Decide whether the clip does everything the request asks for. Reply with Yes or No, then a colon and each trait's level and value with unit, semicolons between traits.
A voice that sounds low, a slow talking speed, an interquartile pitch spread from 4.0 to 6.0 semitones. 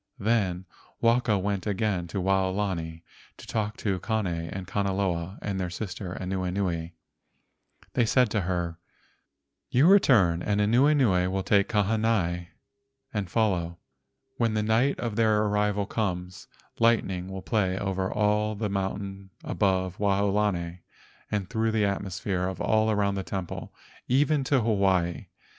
No: low, 100 Hz; slow, 130 wpm; average, 2.8 semitones